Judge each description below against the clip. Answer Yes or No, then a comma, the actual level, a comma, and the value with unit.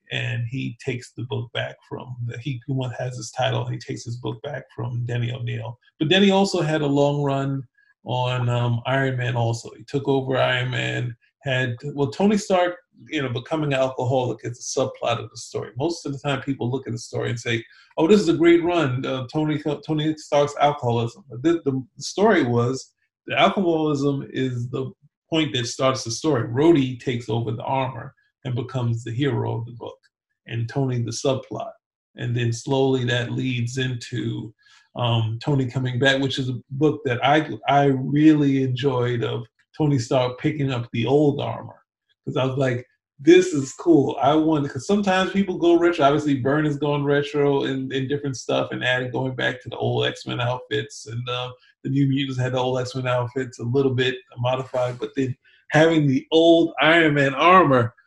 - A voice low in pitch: Yes, low, 130 Hz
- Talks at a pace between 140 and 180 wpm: No, average, 190 wpm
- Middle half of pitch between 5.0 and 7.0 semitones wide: No, average, 3.2 semitones